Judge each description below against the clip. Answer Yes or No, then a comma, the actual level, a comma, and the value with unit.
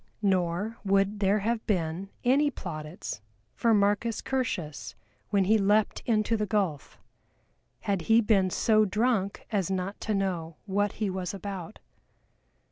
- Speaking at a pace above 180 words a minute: No, slow, 135 wpm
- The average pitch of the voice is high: Yes, high, 200 Hz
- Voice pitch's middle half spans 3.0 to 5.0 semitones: No, narrow, 2.6 semitones